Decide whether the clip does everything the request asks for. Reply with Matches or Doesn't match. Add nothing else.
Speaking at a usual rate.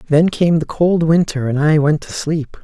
Doesn't match